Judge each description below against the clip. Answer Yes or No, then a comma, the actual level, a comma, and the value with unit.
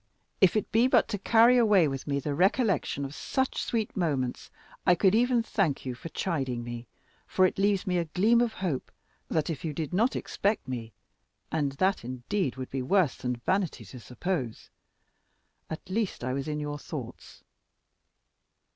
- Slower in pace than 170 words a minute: No, average, 175 wpm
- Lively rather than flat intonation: Yes, wide, 7.3 semitones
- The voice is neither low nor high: Yes, medium, 165 Hz